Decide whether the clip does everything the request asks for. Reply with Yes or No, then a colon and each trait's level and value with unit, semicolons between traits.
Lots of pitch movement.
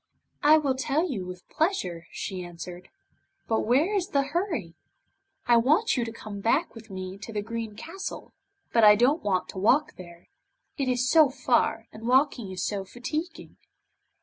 Yes: wide, 7.1 semitones